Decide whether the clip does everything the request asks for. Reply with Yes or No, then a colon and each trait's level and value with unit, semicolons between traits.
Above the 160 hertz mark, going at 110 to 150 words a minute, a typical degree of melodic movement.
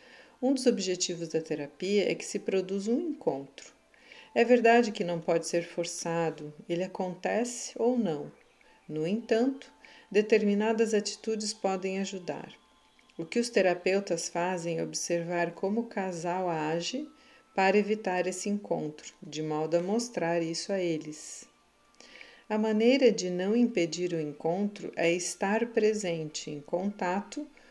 Yes: high, 190 Hz; average, 135 wpm; average, 4.7 semitones